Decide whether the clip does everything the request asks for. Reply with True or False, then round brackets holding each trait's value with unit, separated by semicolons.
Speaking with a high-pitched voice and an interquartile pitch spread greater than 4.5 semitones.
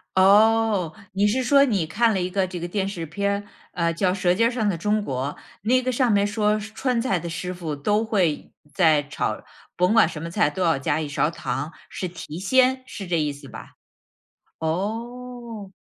True (195 Hz; 4.9 semitones)